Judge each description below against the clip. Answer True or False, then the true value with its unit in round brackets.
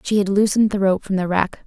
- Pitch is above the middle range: True (195 Hz)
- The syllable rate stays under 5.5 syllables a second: False (6.4 syllables/s)